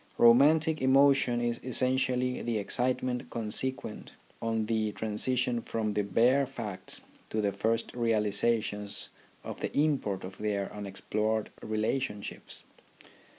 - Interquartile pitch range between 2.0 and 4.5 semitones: Yes, average, 3.3 semitones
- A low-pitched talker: Yes, low, 115 Hz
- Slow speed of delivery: Yes, slow, 110 wpm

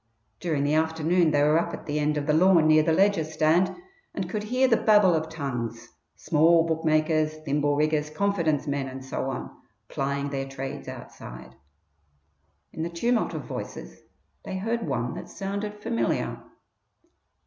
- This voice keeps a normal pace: Yes, average, 160 wpm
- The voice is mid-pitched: Yes, medium, 155 Hz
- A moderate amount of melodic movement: Yes, average, 3.9 semitones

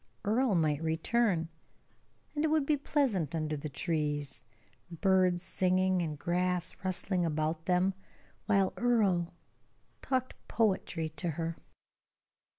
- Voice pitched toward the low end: No, medium, 180 Hz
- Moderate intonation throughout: Yes, average, 4.0 semitones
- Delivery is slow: Yes, slow, 115 wpm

